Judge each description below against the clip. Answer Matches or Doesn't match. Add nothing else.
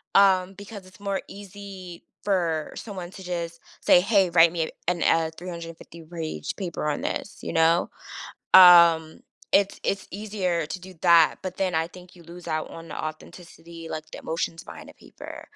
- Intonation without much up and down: Matches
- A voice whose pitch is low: Doesn't match